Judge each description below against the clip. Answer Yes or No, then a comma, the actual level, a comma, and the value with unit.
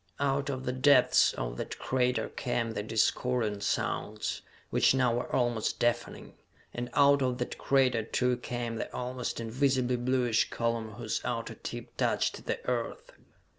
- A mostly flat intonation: Yes, narrow, 1.8 semitones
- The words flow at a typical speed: Yes, average, 150 wpm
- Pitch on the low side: Yes, low, 125 Hz